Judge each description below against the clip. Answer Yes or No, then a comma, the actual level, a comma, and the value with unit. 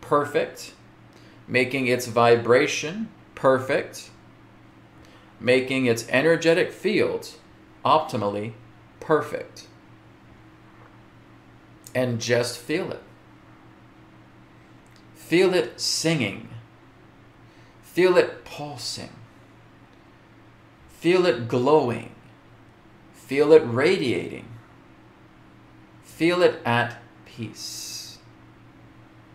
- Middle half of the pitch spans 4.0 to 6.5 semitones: Yes, average, 5.2 semitones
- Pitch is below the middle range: Yes, low, 120 Hz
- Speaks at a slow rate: Yes, slow, 65 wpm